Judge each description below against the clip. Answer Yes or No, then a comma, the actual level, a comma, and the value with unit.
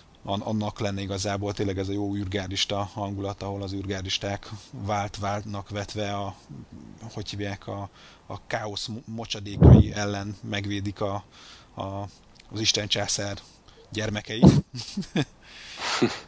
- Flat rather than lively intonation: Yes, narrow, 1.5 semitones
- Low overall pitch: Yes, low, 100 Hz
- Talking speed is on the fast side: No, slow, 105 wpm